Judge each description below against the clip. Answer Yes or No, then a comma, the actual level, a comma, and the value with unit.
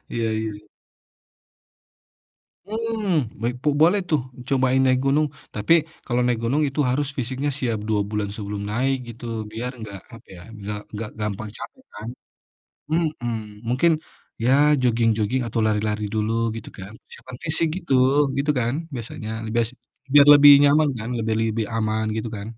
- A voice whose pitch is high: No, low, 120 Hz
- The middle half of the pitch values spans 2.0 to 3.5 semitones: No, average, 4.6 semitones